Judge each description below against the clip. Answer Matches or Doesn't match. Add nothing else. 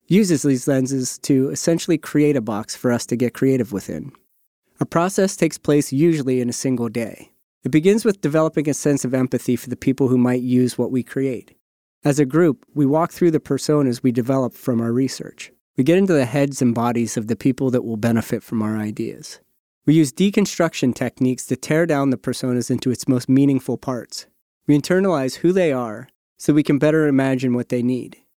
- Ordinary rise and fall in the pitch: Matches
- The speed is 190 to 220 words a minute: Matches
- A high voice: Doesn't match